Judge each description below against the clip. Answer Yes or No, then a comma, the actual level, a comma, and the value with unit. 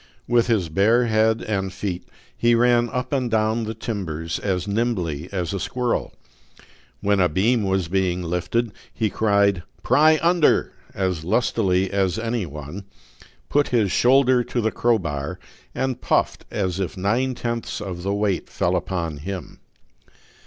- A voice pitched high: No, low, 100 Hz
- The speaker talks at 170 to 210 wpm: No, average, 150 wpm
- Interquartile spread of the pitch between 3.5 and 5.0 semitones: Yes, average, 4.4 semitones